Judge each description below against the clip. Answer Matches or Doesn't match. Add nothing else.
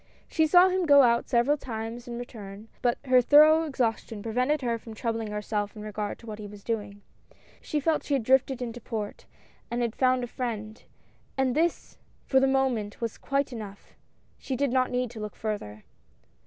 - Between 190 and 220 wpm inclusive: Matches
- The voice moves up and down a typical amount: Matches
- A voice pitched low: Doesn't match